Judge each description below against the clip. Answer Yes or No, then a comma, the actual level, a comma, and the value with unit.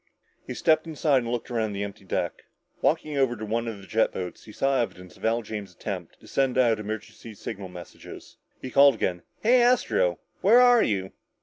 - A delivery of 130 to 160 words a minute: No, average, 200 wpm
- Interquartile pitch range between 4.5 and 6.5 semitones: Yes, wide, 5.4 semitones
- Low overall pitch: Yes, low, 115 Hz